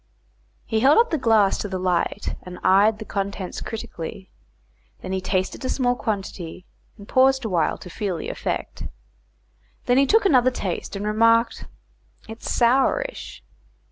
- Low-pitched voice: No, high, 215 Hz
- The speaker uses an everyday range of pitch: Yes, average, 4.7 semitones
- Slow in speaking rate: No, average, 150 wpm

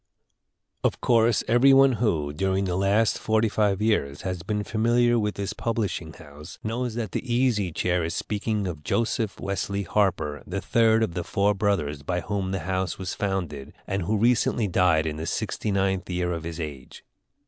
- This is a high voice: No, low, 100 Hz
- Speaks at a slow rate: No, average, 180 wpm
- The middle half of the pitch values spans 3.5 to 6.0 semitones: Yes, average, 4.0 semitones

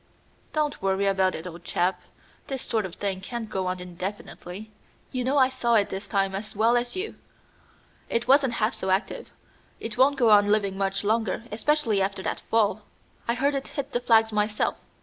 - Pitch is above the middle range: Yes, high, 215 Hz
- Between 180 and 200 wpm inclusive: Yes, average, 190 wpm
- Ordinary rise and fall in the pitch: Yes, average, 4.0 semitones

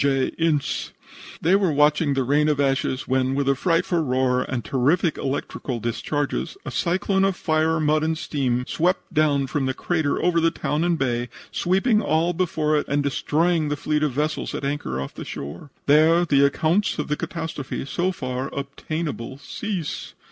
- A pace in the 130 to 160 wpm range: No, average, 175 wpm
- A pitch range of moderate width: Yes, average, 3.4 semitones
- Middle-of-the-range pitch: Yes, medium, 150 Hz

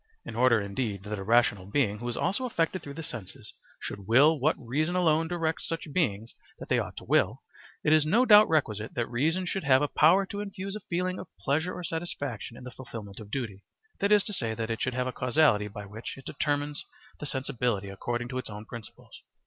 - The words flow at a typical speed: No, fast, 220 wpm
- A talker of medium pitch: No, low, 130 Hz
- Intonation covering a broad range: Yes, wide, 6.5 semitones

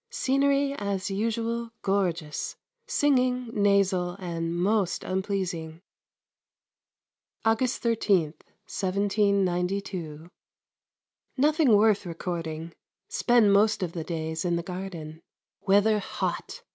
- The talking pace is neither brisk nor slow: No, slow, 90 wpm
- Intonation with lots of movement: No, average, 4.4 semitones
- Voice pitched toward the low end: No, high, 195 Hz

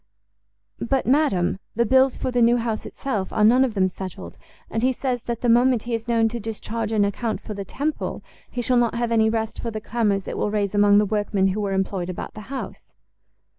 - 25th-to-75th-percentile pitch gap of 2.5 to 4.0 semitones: Yes, average, 2.9 semitones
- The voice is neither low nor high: No, high, 225 Hz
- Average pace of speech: No, fast, 225 wpm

